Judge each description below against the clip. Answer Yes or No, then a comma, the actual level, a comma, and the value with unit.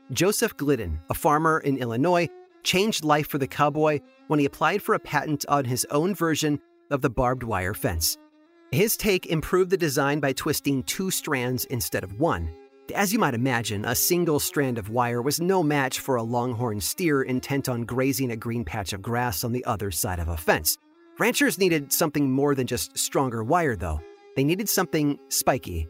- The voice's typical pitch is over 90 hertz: Yes, medium, 140 Hz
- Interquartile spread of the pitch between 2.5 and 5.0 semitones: No, wide, 5.4 semitones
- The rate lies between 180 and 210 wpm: Yes, average, 190 wpm